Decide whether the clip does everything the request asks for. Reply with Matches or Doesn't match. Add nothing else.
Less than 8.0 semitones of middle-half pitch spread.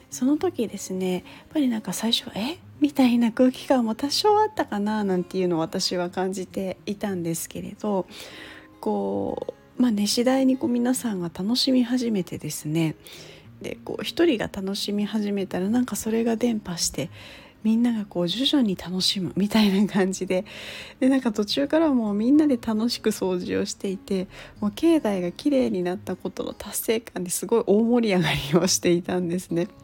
Matches